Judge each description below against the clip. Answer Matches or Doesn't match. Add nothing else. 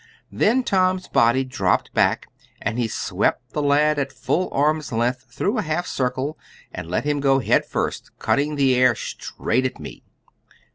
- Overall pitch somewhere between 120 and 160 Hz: Matches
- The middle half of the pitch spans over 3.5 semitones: Doesn't match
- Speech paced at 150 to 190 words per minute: Matches